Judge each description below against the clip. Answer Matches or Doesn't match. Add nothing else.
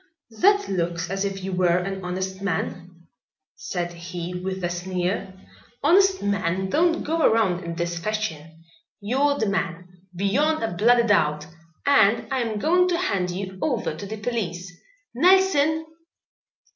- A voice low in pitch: Doesn't match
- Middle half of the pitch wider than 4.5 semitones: Matches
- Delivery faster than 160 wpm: Doesn't match